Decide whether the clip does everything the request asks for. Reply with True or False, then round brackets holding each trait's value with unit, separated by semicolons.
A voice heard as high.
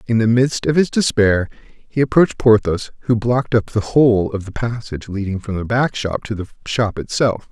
False (110 Hz)